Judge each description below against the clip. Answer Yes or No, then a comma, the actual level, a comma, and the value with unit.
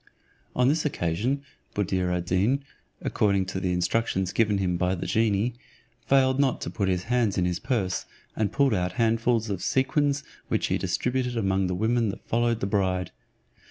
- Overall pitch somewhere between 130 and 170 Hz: No, low, 105 Hz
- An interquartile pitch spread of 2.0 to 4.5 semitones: No, average, 5.0 semitones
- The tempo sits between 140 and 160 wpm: No, average, 175 wpm